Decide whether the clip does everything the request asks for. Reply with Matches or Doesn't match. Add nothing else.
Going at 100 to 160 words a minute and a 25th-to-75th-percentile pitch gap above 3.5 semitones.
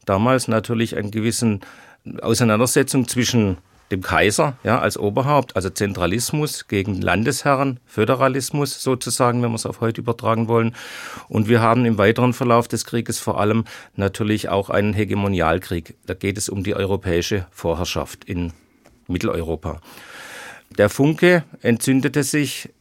Matches